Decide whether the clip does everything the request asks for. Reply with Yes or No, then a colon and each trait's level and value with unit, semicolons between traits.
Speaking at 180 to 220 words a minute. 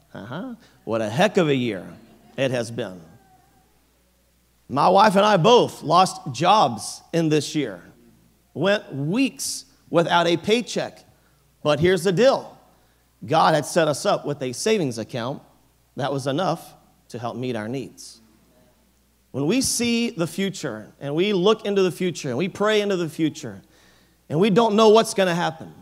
No: average, 165 wpm